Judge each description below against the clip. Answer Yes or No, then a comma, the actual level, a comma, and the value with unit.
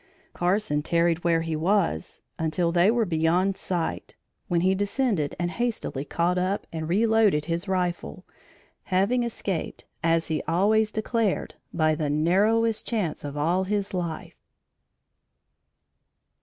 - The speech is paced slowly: Yes, slow, 130 wpm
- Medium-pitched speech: Yes, medium, 180 Hz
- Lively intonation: No, average, 3.9 semitones